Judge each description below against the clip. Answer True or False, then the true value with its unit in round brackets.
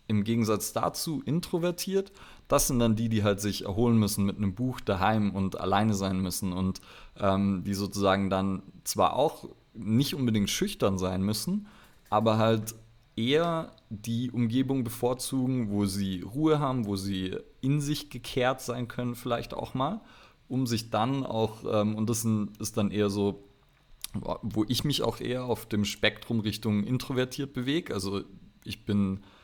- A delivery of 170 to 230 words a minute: False (160 wpm)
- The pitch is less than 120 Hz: True (110 Hz)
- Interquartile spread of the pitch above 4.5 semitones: False (4.1 semitones)